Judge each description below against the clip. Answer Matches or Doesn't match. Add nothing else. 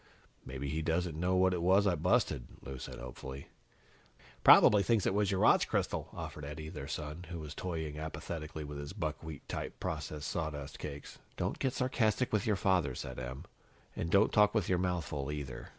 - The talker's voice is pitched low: Matches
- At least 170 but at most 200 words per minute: Matches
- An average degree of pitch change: Matches